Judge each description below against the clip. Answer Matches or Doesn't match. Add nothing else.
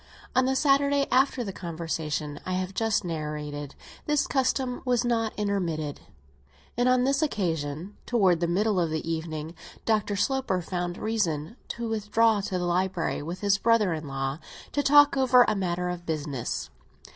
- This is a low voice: Doesn't match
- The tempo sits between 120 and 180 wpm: Matches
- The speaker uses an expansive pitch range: Matches